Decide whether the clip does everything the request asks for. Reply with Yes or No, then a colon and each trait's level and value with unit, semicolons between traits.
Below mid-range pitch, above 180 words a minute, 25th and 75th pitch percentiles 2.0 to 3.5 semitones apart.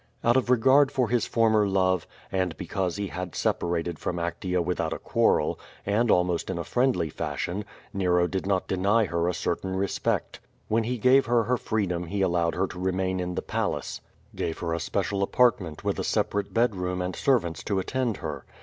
No: very low, 95 Hz; average, 195 wpm; average, 4.0 semitones